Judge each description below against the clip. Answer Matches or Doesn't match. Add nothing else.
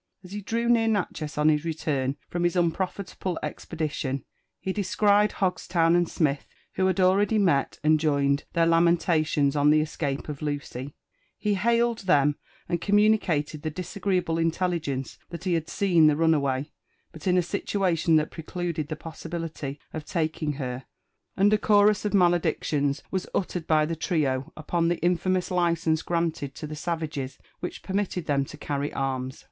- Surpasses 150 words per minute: Matches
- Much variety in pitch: Doesn't match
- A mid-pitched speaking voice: Matches